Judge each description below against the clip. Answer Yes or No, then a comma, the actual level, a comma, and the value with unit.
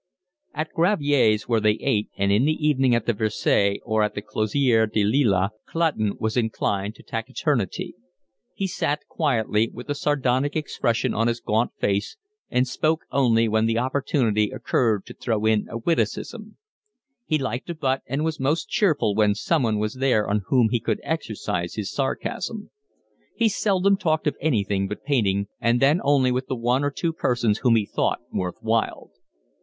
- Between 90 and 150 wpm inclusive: No, average, 175 wpm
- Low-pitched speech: Yes, low, 120 Hz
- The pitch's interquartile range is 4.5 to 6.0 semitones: Yes, average, 5.1 semitones